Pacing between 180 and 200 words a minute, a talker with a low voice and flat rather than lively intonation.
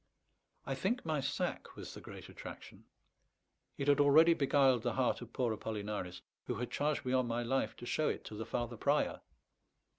No: average, 185 wpm; low, 130 Hz; average, 3.6 semitones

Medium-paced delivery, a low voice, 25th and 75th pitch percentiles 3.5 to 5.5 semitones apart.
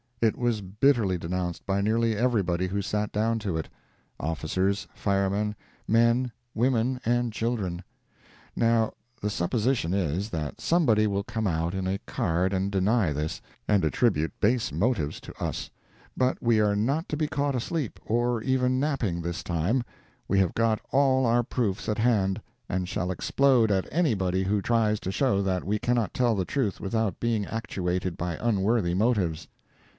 Yes: average, 160 wpm; low, 105 Hz; average, 4.3 semitones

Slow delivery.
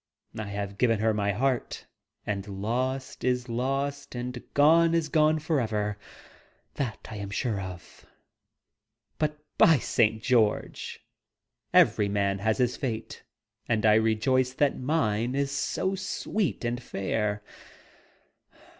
Yes: slow, 125 wpm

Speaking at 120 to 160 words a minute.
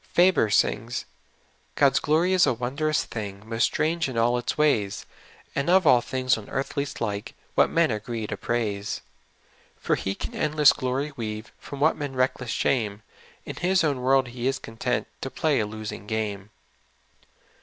No: average, 175 wpm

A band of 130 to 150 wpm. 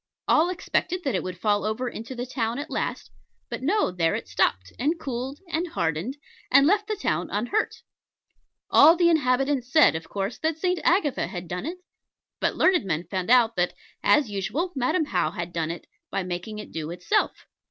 No: average, 190 wpm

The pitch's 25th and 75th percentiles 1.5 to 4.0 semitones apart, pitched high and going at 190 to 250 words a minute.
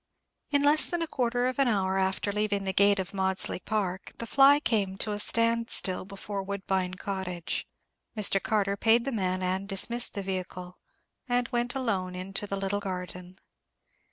No: average, 3.5 semitones; high, 200 Hz; average, 175 wpm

